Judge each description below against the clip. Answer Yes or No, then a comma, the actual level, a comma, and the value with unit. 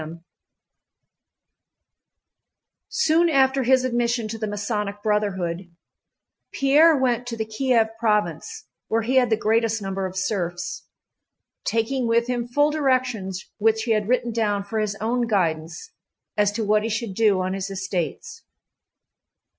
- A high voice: Yes, high, 220 Hz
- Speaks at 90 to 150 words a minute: Yes, average, 145 wpm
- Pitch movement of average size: Yes, average, 3.7 semitones